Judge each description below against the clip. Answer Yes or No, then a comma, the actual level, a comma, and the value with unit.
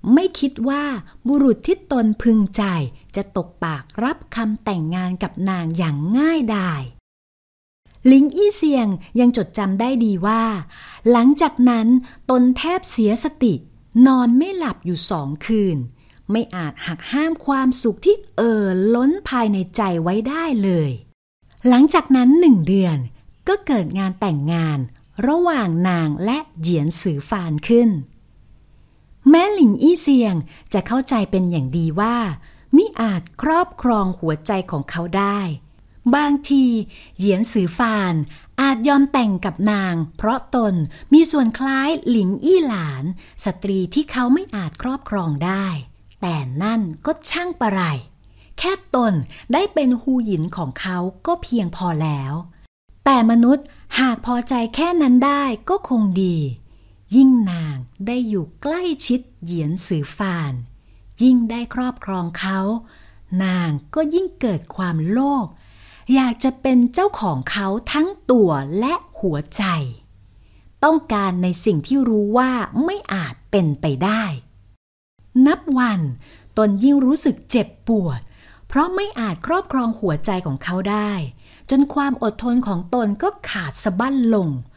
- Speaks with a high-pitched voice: Yes, high, 215 Hz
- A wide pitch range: Yes, wide, 7.6 semitones